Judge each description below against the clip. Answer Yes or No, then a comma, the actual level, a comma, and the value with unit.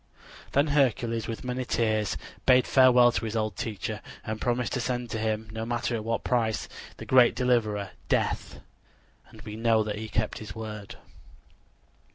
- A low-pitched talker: Yes, low, 115 Hz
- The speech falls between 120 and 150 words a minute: No, average, 170 wpm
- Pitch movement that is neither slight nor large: No, narrow, 2.2 semitones